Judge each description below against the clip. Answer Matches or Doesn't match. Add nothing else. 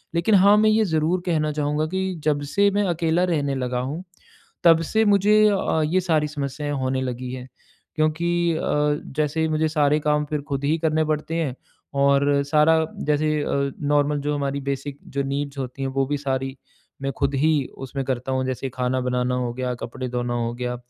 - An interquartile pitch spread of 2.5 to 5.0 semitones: Matches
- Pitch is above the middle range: Doesn't match